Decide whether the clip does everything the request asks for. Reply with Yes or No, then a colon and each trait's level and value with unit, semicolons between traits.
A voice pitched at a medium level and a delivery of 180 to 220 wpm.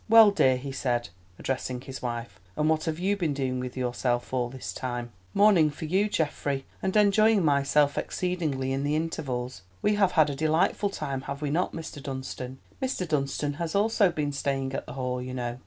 Yes: medium, 145 Hz; average, 195 wpm